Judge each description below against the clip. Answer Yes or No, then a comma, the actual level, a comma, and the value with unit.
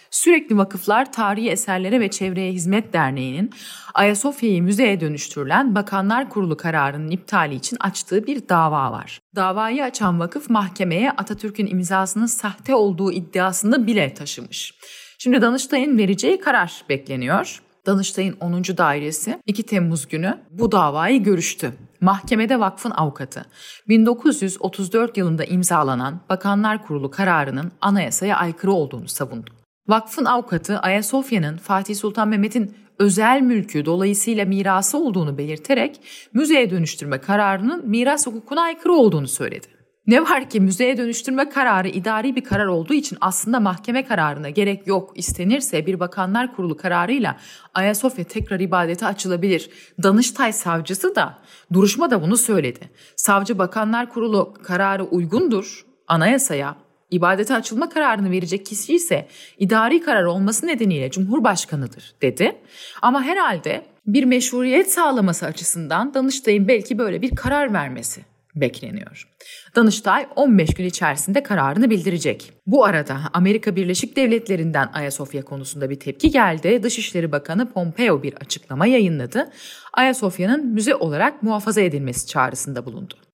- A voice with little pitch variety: No, wide, 5.4 semitones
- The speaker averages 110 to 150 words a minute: Yes, average, 120 wpm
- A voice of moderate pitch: No, high, 200 Hz